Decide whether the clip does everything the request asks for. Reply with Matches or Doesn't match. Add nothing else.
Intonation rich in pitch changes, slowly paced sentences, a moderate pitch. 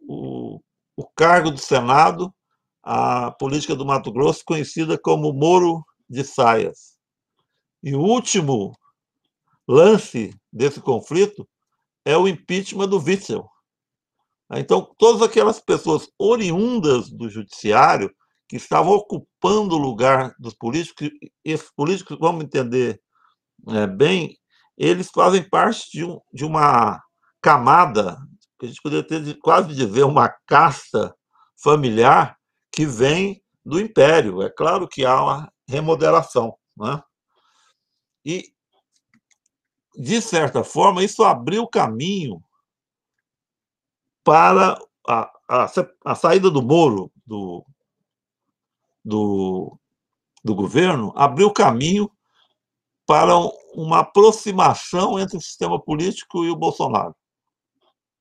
Matches